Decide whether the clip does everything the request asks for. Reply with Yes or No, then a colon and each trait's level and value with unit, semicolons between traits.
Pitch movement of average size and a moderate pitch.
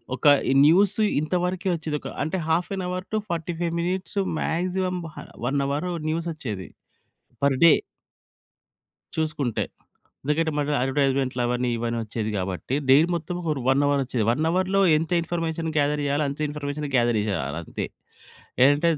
Yes: average, 4.2 semitones; medium, 150 Hz